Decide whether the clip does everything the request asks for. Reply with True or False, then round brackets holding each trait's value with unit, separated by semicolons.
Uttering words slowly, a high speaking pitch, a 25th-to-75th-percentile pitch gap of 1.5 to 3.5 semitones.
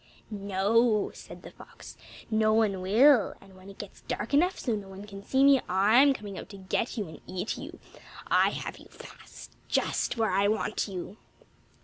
False (190 wpm; 205 Hz; 2.9 semitones)